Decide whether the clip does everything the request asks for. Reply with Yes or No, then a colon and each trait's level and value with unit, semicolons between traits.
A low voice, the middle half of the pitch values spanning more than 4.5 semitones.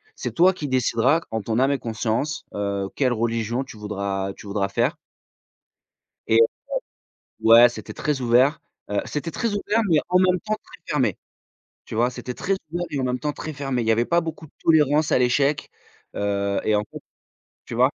Yes: low, 125 Hz; wide, 5.5 semitones